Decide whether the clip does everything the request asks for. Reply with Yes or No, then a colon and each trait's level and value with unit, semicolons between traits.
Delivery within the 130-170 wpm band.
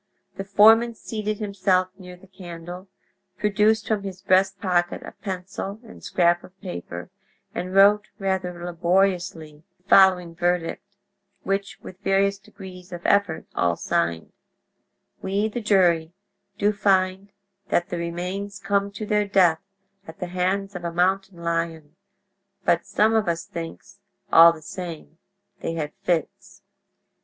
Yes: average, 140 wpm